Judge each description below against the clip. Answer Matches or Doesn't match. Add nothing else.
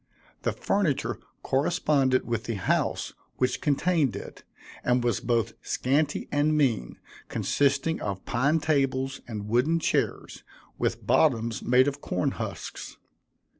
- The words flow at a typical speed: Doesn't match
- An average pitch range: Matches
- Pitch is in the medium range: Doesn't match